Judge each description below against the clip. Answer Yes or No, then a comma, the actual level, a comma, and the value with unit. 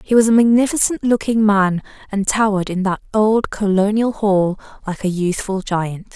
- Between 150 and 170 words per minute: Yes, average, 165 wpm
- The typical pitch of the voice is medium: No, high, 205 Hz